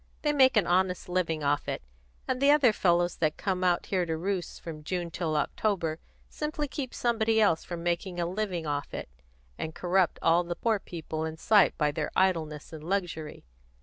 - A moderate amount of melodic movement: Yes, average, 4.0 semitones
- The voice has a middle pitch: Yes, medium, 175 Hz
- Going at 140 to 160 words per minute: No, average, 190 wpm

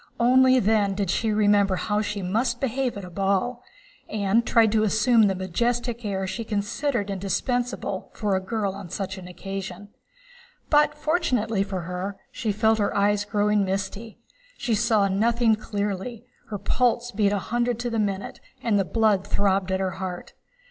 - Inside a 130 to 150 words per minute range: No, average, 170 wpm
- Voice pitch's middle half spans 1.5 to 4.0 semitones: Yes, average, 3.2 semitones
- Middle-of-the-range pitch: No, high, 210 Hz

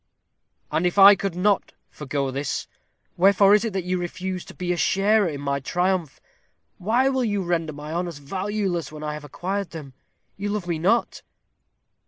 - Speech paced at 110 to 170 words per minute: No, average, 180 wpm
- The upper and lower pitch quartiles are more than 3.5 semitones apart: Yes, average, 4.2 semitones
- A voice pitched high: No, medium, 180 Hz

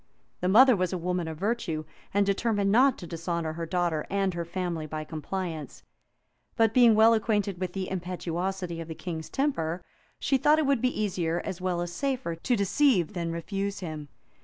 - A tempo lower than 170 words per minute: No, average, 185 wpm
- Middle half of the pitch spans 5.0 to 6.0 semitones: No, average, 4.2 semitones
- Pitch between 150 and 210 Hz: Yes, medium, 185 Hz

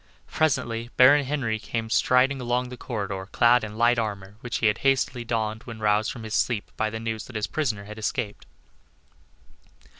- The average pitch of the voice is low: Yes, low, 115 Hz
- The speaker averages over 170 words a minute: Yes, average, 180 wpm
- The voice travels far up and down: No, average, 2.7 semitones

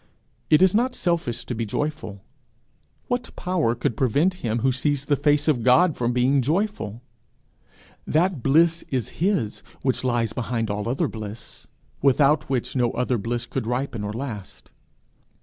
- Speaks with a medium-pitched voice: No, low, 130 Hz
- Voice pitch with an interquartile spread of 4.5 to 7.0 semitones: Yes, average, 4.8 semitones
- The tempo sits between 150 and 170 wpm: Yes, average, 155 wpm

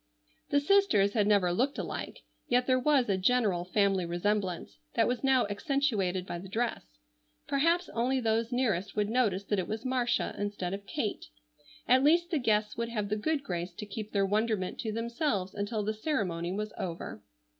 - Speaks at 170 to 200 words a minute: Yes, average, 180 wpm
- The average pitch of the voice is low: No, high, 215 Hz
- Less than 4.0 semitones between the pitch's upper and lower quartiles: No, average, 4.4 semitones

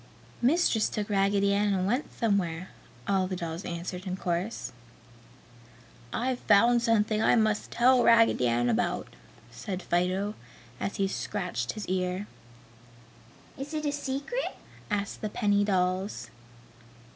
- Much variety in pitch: No, average, 3.8 semitones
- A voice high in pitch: Yes, high, 200 Hz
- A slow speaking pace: Yes, slow, 130 wpm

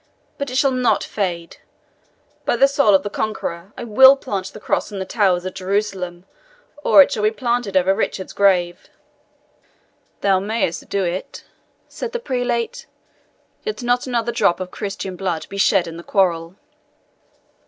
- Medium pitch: No, high, 200 Hz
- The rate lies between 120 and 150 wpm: No, average, 165 wpm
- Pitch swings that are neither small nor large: Yes, average, 4.5 semitones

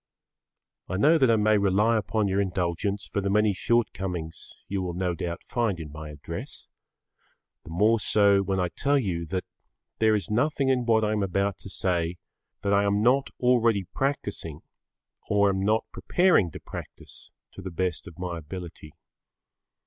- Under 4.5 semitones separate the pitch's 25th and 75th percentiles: Yes, average, 3.6 semitones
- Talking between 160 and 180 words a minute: Yes, average, 175 wpm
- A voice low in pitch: Yes, low, 100 Hz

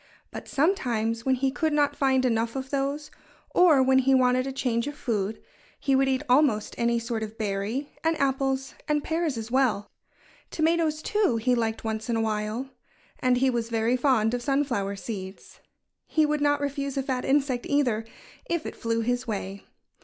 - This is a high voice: Yes, very high, 255 Hz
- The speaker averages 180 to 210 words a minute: Yes, average, 185 wpm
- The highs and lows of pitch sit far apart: No, average, 3.6 semitones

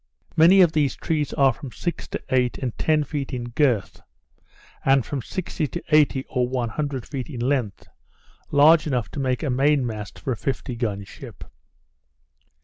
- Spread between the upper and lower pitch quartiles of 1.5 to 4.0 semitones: Yes, average, 3.4 semitones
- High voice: No, low, 135 Hz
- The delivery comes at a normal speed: Yes, average, 175 wpm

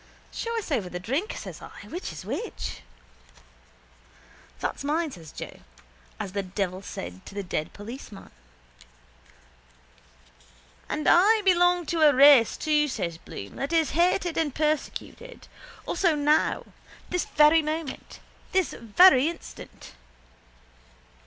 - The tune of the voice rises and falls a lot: Yes, wide, 8.7 semitones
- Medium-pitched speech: No, very high, 300 Hz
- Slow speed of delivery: Yes, slow, 125 wpm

